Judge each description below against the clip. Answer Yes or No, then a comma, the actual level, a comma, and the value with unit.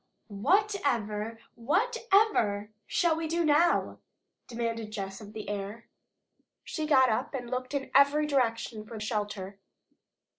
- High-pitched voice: Yes, high, 240 Hz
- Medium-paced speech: No, slow, 120 wpm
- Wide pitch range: Yes, wide, 6.2 semitones